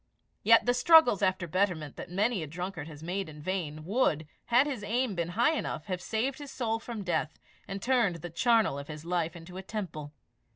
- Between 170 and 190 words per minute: No, fast, 205 wpm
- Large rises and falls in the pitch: Yes, wide, 5.8 semitones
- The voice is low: No, high, 190 Hz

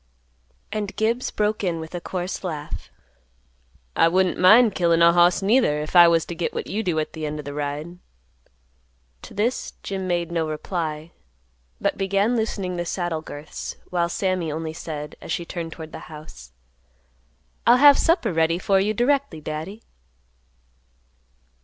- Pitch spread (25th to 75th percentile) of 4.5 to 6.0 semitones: No, average, 3.8 semitones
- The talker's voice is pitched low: No, medium, 175 Hz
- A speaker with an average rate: Yes, average, 165 wpm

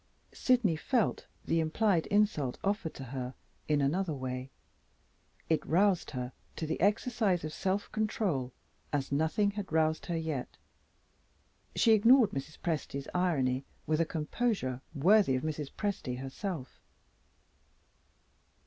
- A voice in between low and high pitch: Yes, medium, 160 Hz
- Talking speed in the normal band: No, slow, 125 wpm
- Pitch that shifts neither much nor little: No, wide, 6.6 semitones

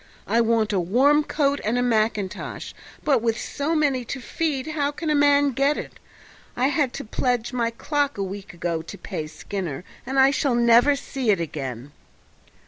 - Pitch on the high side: Yes, high, 245 Hz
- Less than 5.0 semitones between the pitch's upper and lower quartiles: No, wide, 5.5 semitones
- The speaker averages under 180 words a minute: No, average, 185 wpm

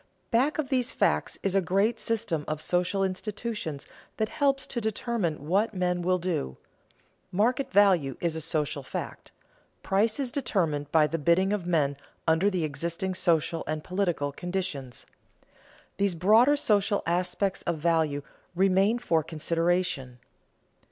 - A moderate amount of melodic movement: Yes, average, 4.5 semitones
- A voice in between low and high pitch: Yes, medium, 180 Hz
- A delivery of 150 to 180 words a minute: No, average, 140 wpm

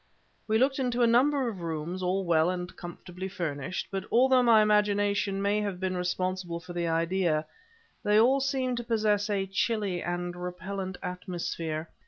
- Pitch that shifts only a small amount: No, average, 3.5 semitones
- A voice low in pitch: No, high, 190 Hz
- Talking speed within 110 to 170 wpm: Yes, average, 165 wpm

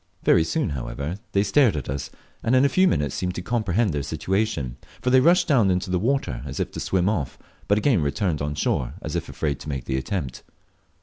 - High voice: No, very low, 90 Hz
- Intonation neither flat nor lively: No, wide, 7.7 semitones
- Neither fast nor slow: No, fast, 225 wpm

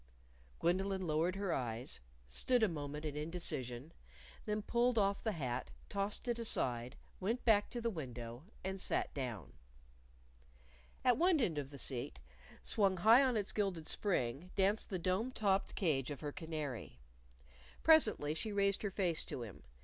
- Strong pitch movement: Yes, wide, 6.8 semitones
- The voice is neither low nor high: Yes, medium, 180 Hz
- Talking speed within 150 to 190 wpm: Yes, average, 155 wpm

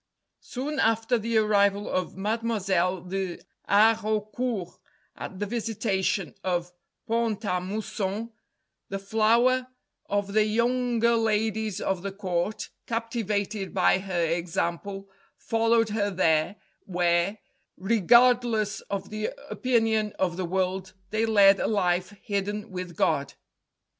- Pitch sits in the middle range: No, high, 205 Hz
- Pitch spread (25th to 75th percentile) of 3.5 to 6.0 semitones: No, average, 3.0 semitones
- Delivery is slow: Yes, slow, 115 wpm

